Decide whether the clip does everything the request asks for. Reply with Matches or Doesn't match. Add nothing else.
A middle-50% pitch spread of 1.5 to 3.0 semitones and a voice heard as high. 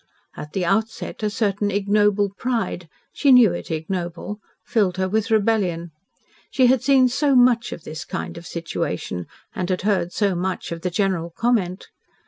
Doesn't match